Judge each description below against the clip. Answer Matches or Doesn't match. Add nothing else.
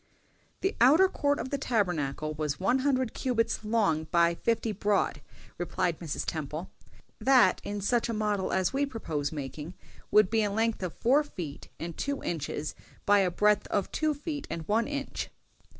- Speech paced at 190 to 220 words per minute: Doesn't match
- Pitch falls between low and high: Doesn't match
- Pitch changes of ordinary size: Doesn't match